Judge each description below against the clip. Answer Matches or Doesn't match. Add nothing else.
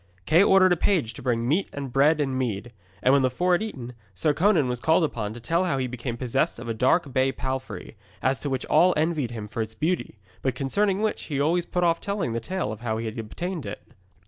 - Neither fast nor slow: Doesn't match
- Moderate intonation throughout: Doesn't match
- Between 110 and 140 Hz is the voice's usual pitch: Matches